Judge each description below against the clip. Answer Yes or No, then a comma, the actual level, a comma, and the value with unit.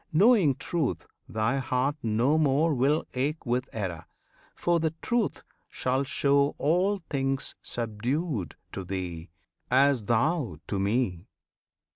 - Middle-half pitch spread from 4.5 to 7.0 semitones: Yes, wide, 5.6 semitones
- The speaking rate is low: Yes, slow, 120 wpm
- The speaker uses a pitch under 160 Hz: Yes, low, 135 Hz